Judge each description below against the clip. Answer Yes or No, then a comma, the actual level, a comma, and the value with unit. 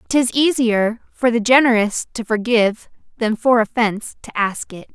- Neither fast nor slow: Yes, average, 160 wpm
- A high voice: Yes, high, 230 Hz